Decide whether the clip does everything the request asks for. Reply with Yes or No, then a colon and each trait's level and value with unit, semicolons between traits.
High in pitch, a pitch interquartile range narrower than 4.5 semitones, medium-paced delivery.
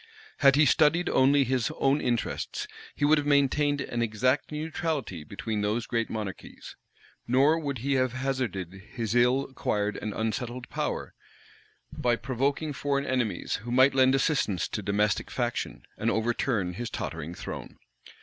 No: low, 125 Hz; average, 4.0 semitones; average, 150 wpm